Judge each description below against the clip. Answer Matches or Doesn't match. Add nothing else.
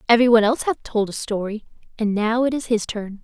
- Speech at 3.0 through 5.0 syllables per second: Doesn't match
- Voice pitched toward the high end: Matches